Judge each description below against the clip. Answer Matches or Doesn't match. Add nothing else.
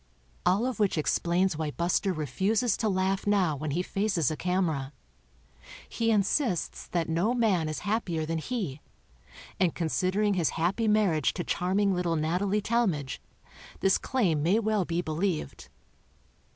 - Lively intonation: Doesn't match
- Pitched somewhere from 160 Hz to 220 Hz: Matches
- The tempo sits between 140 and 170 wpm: Matches